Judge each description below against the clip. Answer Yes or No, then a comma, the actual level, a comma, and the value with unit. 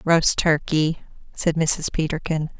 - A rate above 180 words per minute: No, slow, 115 wpm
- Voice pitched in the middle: Yes, medium, 160 Hz